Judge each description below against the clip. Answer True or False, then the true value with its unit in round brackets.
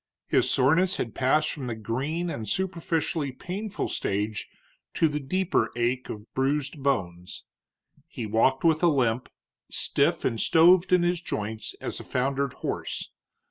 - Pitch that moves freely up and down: True (6.4 semitones)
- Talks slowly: False (145 wpm)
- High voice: False (140 Hz)